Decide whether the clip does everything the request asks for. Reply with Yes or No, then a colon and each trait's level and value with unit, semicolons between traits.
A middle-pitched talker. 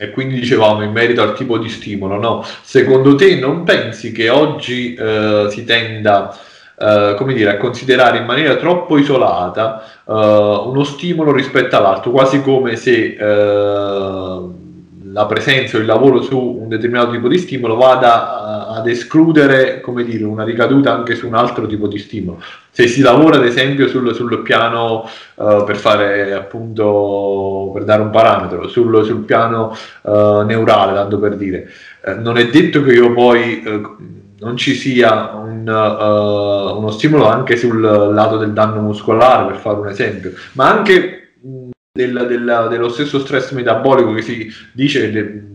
No: low, 115 Hz